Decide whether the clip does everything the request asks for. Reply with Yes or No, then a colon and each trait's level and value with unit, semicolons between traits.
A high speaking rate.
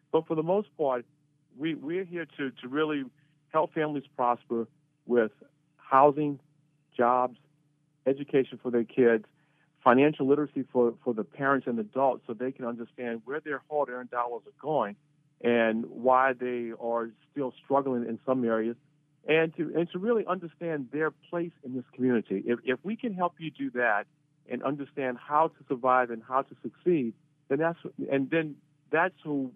No: average, 165 wpm